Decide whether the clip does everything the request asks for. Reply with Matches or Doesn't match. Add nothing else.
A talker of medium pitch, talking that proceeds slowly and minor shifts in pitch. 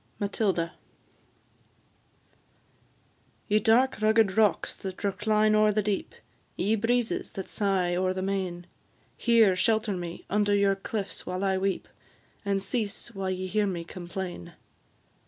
Doesn't match